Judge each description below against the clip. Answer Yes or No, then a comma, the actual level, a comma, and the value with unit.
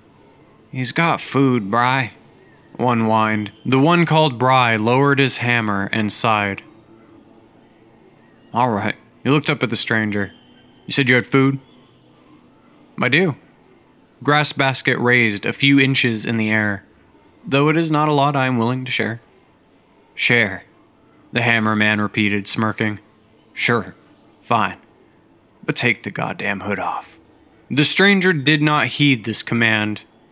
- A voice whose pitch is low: Yes, low, 120 Hz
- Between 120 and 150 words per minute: Yes, average, 140 wpm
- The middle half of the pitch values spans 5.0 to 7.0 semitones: No, average, 4.1 semitones